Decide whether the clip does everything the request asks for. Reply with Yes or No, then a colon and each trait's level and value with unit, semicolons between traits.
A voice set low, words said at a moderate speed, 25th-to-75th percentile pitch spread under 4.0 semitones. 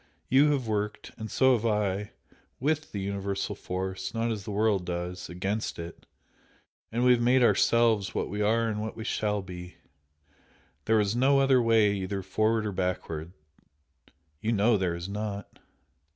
Yes: low, 105 Hz; average, 165 wpm; average, 3.2 semitones